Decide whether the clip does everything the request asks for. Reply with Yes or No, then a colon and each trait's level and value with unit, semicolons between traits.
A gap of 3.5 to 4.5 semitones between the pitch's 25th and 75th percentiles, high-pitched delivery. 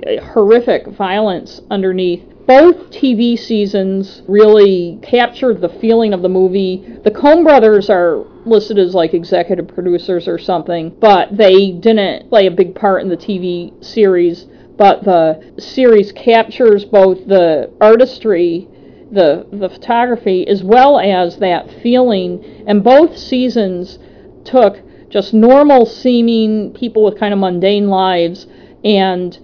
Yes: average, 3.9 semitones; high, 205 Hz